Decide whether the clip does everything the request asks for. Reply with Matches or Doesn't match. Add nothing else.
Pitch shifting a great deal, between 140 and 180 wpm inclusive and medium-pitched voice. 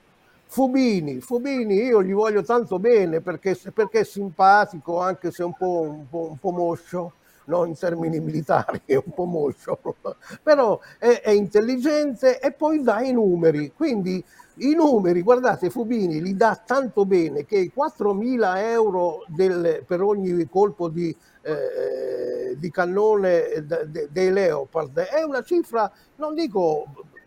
Doesn't match